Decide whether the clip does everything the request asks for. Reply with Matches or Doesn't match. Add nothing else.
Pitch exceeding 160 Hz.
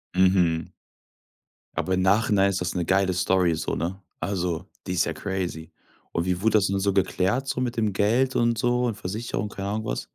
Doesn't match